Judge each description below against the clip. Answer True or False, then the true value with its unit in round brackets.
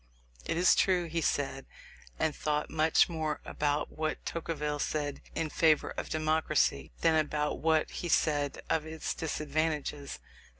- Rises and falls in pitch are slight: True (1.4 semitones)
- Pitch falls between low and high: True (155 Hz)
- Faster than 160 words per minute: False (140 wpm)